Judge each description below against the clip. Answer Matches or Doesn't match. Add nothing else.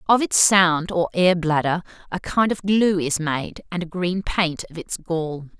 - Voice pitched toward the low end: Doesn't match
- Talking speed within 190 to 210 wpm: Matches